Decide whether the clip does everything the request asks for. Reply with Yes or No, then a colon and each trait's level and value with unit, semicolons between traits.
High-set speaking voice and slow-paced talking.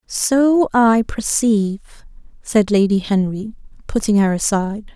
Yes: high, 215 Hz; slow, 110 wpm